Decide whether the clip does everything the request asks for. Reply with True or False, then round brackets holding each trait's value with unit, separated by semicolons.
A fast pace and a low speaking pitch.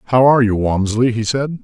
True (220 wpm; 120 Hz)